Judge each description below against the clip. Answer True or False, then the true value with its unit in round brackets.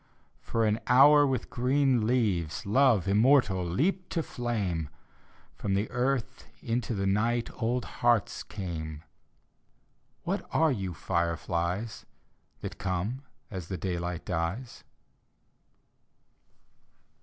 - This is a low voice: True (105 Hz)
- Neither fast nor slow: False (100 wpm)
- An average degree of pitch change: False (5.9 semitones)